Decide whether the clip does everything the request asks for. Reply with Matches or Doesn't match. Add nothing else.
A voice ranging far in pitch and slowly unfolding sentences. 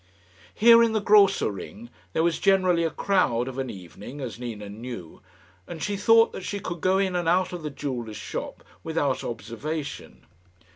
Doesn't match